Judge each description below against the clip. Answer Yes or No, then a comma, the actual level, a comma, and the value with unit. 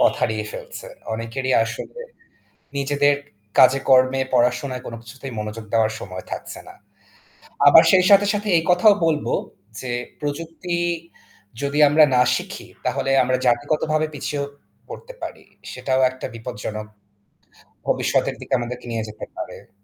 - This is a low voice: Yes, low, 130 Hz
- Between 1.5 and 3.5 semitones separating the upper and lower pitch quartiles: No, average, 4.2 semitones